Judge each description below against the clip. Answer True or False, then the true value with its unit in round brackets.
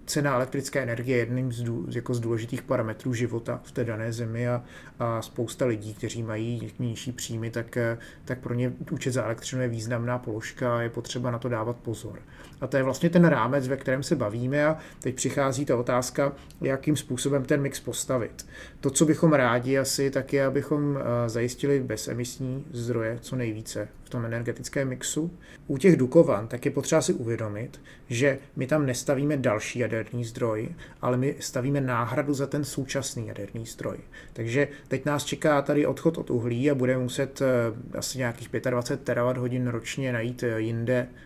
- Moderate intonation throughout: True (3.0 semitones)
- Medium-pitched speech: False (125 Hz)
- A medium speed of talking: False (175 wpm)